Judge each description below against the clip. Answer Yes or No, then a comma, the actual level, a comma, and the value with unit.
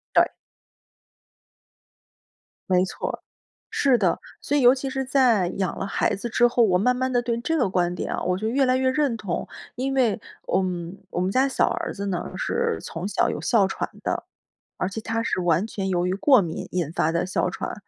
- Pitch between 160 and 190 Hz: No, high, 215 Hz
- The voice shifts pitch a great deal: Yes, wide, 5.9 semitones